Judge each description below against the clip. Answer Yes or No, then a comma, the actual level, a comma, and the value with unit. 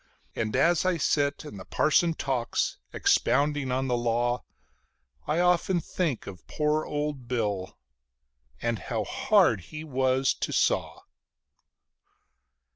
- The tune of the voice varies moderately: Yes, average, 4.4 semitones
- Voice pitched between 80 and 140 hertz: Yes, low, 135 Hz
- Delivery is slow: Yes, slow, 120 wpm